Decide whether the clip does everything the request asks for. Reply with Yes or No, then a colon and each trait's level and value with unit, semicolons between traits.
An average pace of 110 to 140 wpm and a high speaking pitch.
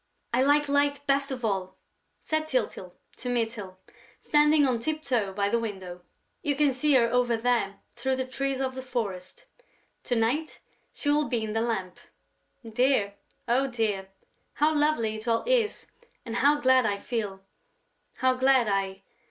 No: average, 165 wpm; high, 245 Hz